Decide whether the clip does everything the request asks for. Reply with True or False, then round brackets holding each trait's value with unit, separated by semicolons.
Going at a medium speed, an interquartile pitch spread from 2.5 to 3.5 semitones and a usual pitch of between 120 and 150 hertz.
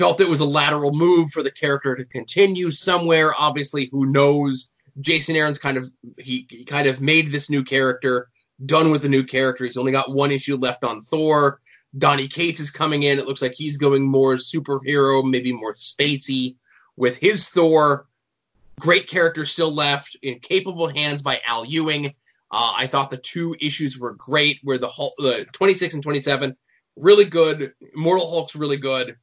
True (185 wpm; 2.8 semitones; 140 Hz)